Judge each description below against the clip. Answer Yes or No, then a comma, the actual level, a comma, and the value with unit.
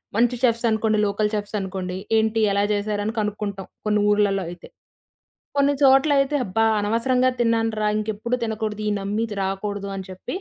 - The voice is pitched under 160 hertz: No, high, 215 Hz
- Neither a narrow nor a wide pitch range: No, narrow, 2.2 semitones